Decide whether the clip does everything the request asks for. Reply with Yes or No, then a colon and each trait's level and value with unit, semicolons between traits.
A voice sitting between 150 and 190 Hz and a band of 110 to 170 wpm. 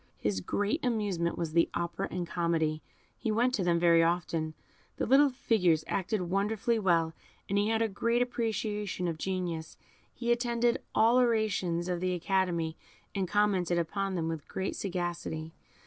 Yes: medium, 185 Hz; average, 165 wpm